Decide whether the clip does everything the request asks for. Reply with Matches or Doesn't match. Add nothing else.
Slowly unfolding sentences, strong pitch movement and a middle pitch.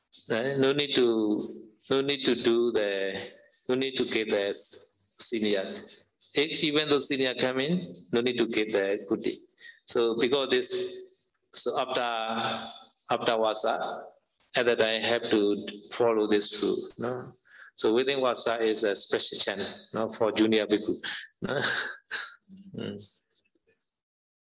Doesn't match